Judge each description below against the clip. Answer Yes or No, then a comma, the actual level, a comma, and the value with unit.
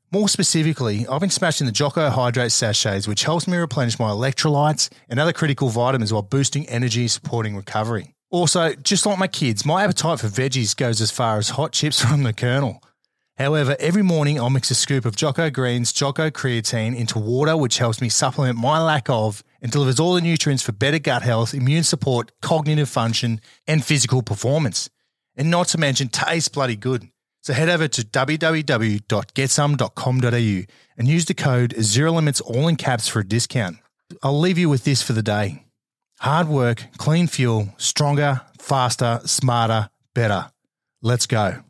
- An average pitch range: Yes, average, 4.5 semitones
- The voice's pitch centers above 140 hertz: No, low, 135 Hz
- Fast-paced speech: No, average, 175 wpm